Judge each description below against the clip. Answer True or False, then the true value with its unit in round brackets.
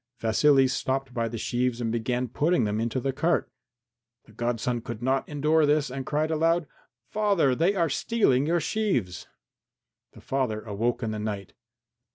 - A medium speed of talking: True (165 wpm)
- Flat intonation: False (4.9 semitones)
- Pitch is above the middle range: False (130 Hz)